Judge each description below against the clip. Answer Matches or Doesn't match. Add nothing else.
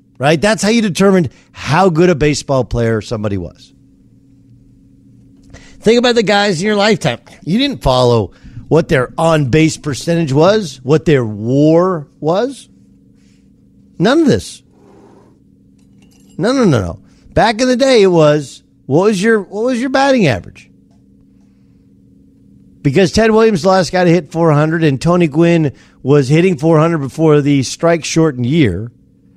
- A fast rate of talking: Doesn't match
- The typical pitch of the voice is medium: Matches